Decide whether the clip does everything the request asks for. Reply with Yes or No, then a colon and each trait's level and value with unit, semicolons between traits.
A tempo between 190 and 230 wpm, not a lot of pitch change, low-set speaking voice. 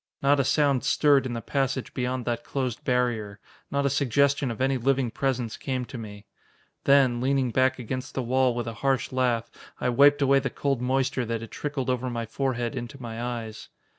Yes: average, 195 wpm; narrow, 2.3 semitones; low, 130 Hz